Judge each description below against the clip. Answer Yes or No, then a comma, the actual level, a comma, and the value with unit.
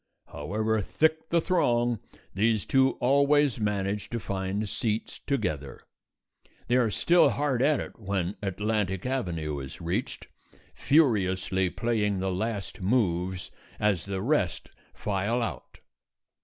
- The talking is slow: Yes, slow, 120 wpm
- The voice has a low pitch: Yes, low, 105 Hz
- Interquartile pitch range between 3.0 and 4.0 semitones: No, average, 4.7 semitones